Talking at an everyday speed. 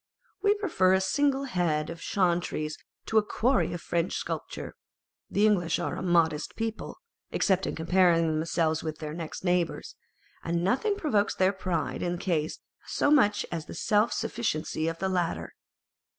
Yes: average, 165 wpm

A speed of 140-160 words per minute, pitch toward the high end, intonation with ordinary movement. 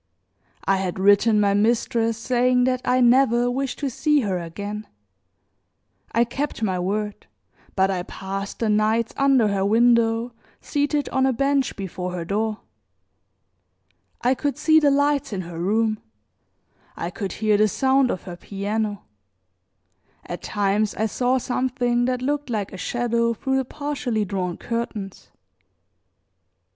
Yes: average, 145 wpm; high, 225 Hz; average, 4.1 semitones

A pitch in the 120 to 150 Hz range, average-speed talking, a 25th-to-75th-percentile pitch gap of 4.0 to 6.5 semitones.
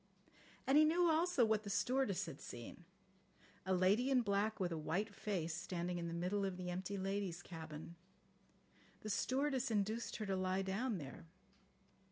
No: high, 195 Hz; average, 170 wpm; average, 4.3 semitones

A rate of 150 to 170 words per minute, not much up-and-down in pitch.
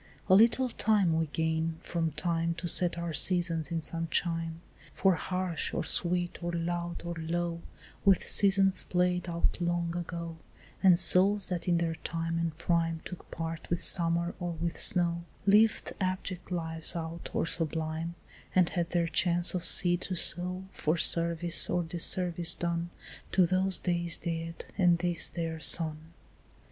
Yes: average, 155 wpm; narrow, 1.3 semitones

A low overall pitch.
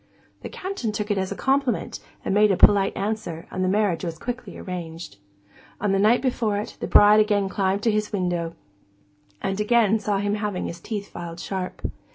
No: high, 205 Hz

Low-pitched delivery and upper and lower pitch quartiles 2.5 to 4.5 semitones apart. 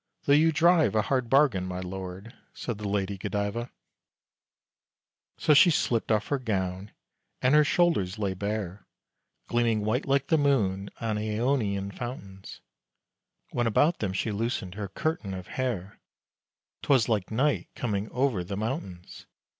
No: low, 110 Hz; average, 5.2 semitones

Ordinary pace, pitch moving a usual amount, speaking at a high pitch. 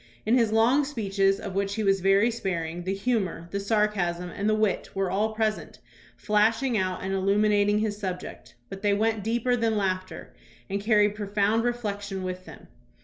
No: average, 175 wpm; narrow, 2.2 semitones; high, 205 Hz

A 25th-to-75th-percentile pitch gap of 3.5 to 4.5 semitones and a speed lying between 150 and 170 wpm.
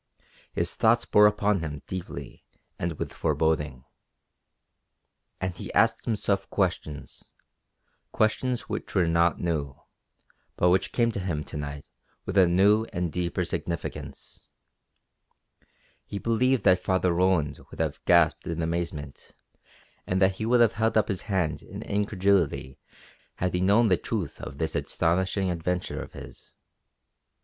No: average, 3.8 semitones; average, 140 wpm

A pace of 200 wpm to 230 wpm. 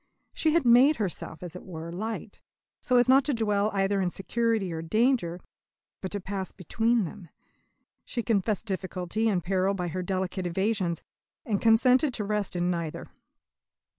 No: average, 165 wpm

